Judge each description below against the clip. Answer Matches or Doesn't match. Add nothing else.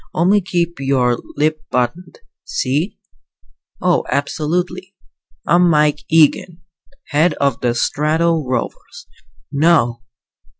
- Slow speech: Matches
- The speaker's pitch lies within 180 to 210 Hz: Doesn't match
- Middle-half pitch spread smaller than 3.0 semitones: Doesn't match